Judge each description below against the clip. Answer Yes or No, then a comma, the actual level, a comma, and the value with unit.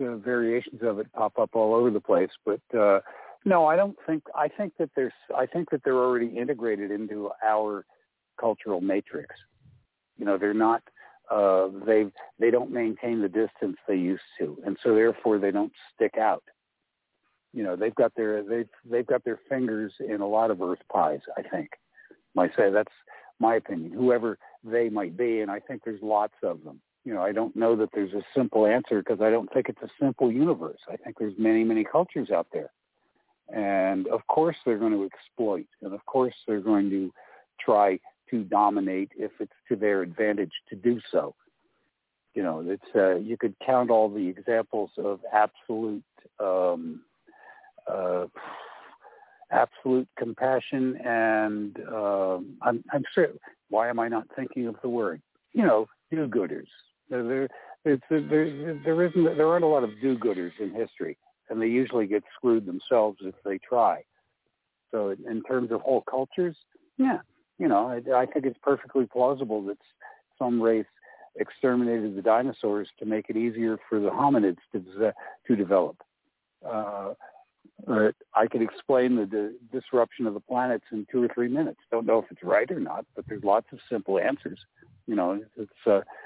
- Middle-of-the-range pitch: No, low, 115 Hz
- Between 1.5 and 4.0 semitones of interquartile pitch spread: Yes, average, 3.4 semitones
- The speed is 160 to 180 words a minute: Yes, average, 175 wpm